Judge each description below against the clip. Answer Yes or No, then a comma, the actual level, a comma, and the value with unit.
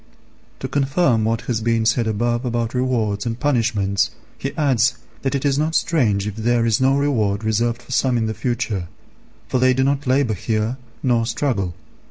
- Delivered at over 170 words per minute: Yes, average, 185 wpm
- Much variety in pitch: No, average, 3.2 semitones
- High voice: No, low, 120 Hz